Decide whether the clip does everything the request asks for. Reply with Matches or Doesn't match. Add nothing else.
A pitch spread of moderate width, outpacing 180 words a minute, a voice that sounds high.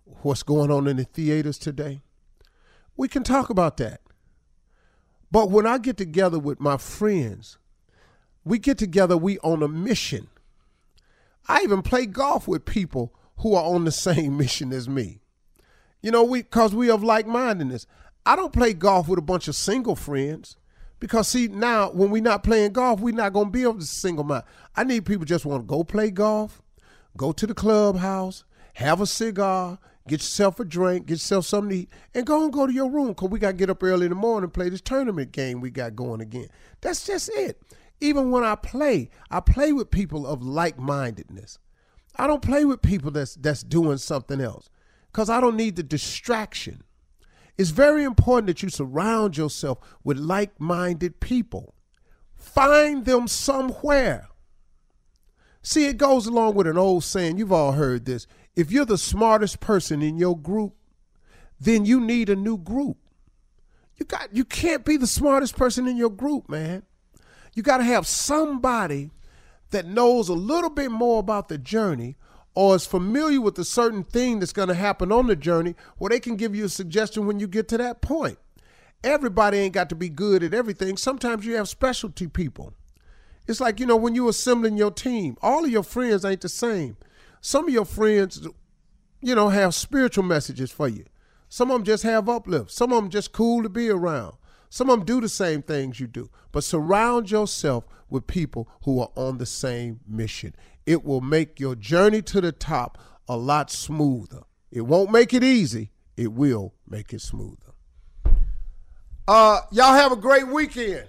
Doesn't match